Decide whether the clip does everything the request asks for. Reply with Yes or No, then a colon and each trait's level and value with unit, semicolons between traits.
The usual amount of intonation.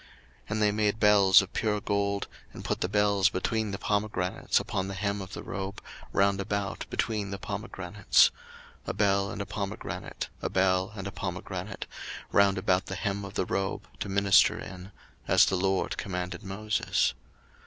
No: narrow, 1.3 semitones